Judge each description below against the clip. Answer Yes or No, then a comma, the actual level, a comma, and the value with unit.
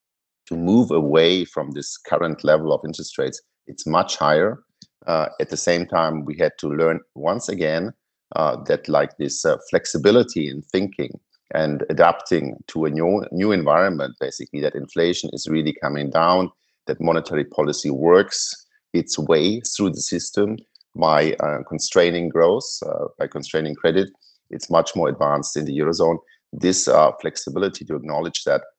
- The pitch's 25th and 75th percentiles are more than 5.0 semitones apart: Yes, wide, 5.5 semitones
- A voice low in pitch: Yes, very low, 85 Hz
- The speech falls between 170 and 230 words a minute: No, average, 160 wpm